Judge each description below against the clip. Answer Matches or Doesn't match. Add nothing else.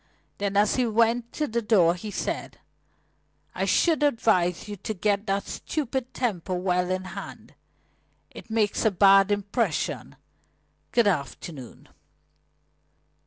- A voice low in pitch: Doesn't match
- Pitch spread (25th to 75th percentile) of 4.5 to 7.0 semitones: Doesn't match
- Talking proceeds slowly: Matches